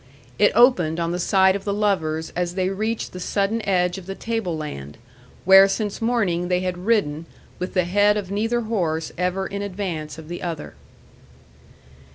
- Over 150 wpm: Yes, average, 175 wpm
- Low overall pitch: No, medium, 185 Hz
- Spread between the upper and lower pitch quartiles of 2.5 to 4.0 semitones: Yes, average, 3.0 semitones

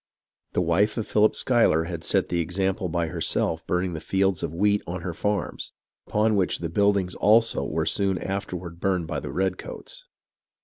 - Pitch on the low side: Yes, very low, 95 Hz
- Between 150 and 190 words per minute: Yes, average, 175 wpm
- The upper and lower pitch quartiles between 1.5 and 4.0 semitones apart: Yes, average, 3.2 semitones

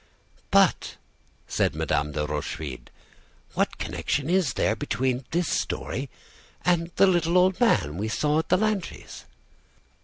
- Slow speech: Yes, slow, 130 wpm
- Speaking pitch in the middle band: Yes, medium, 150 Hz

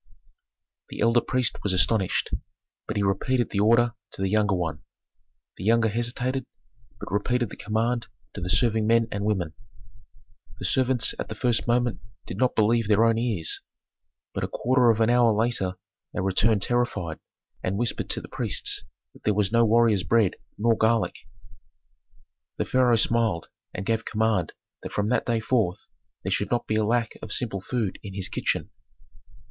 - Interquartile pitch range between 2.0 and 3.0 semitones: Yes, average, 2.7 semitones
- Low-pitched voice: Yes, low, 110 Hz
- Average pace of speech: Yes, average, 175 wpm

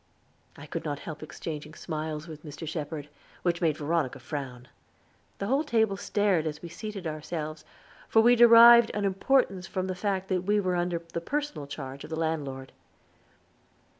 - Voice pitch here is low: No, medium, 170 Hz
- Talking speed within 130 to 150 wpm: No, average, 165 wpm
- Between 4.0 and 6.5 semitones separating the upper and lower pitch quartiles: Yes, average, 4.8 semitones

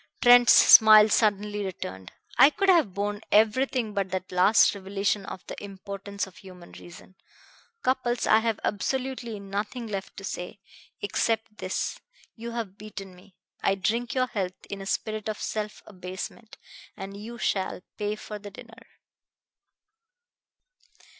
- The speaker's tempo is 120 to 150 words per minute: Yes, average, 140 wpm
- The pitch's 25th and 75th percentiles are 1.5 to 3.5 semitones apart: Yes, narrow, 2.6 semitones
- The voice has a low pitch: No, high, 205 Hz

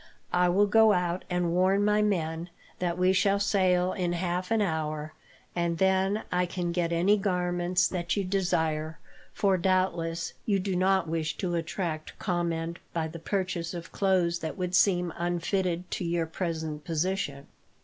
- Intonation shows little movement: Yes, narrow, 2.1 semitones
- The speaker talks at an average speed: Yes, average, 160 wpm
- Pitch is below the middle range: No, medium, 180 Hz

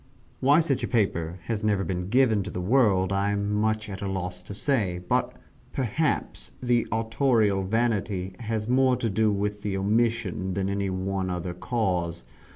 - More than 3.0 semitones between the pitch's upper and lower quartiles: Yes, average, 3.4 semitones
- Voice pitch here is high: No, low, 105 Hz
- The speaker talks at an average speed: Yes, average, 175 wpm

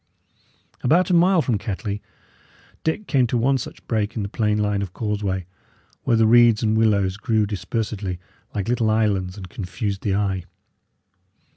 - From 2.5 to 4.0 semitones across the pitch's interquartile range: Yes, average, 2.8 semitones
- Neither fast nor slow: Yes, average, 160 wpm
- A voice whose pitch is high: No, low, 105 Hz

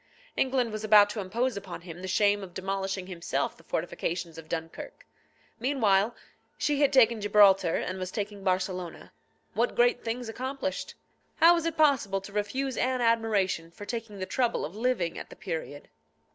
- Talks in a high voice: Yes, high, 205 Hz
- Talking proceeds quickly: No, average, 170 wpm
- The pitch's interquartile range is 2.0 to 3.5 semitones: No, average, 4.8 semitones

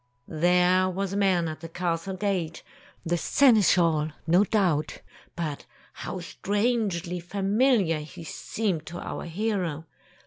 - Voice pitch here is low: No, medium, 180 Hz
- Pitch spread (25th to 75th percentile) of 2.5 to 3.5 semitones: Yes, average, 3.2 semitones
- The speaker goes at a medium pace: No, slow, 125 wpm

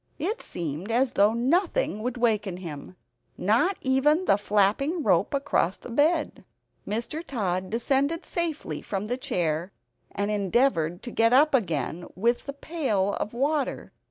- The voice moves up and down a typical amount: No, wide, 6.4 semitones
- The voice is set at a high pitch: Yes, high, 235 Hz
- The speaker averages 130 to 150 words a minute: Yes, average, 145 wpm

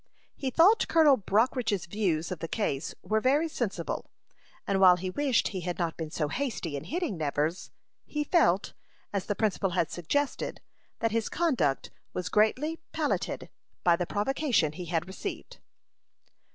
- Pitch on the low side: No, high, 205 Hz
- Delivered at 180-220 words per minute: No, average, 155 wpm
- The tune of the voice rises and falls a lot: Yes, wide, 7.7 semitones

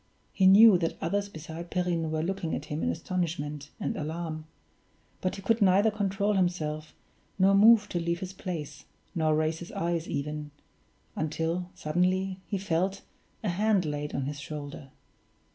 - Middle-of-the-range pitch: Yes, medium, 170 Hz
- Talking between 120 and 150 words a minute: No, average, 160 wpm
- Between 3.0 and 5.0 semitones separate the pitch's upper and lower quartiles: Yes, average, 3.7 semitones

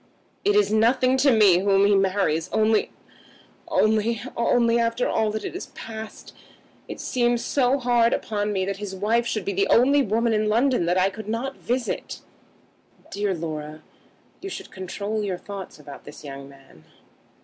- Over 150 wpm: Yes, average, 160 wpm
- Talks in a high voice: Yes, high, 215 Hz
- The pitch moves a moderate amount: Yes, average, 3.7 semitones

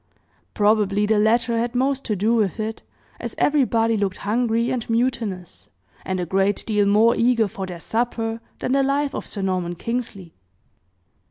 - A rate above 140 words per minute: Yes, average, 165 wpm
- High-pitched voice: Yes, high, 220 Hz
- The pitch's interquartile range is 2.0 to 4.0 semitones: Yes, average, 3.1 semitones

